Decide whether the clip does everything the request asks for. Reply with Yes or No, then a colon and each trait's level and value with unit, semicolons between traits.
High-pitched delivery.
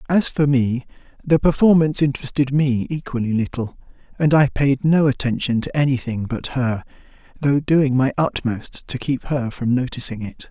No: low, 135 Hz